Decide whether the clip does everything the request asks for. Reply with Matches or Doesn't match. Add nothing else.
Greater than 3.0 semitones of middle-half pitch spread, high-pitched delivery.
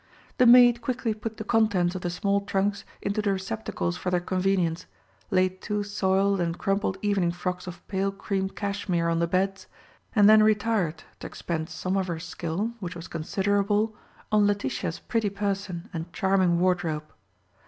Doesn't match